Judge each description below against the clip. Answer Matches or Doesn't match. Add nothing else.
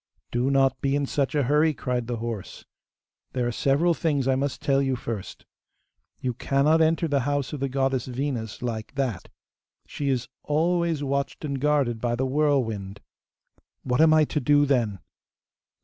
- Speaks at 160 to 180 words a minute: Matches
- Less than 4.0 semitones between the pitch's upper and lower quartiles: Matches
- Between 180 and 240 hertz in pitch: Doesn't match